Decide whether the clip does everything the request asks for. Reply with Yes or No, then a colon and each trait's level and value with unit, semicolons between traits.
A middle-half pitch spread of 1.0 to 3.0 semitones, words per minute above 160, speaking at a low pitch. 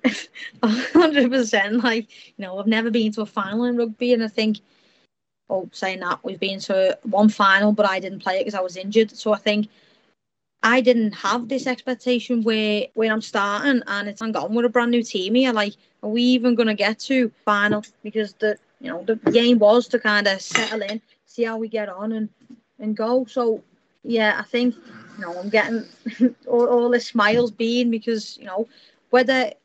No: average, 2.7 semitones; average, 200 wpm; high, 225 Hz